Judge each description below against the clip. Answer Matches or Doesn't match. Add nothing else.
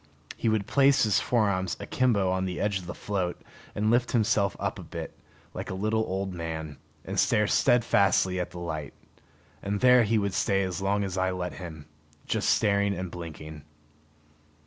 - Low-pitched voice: Matches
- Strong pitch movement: Doesn't match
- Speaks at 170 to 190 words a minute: Matches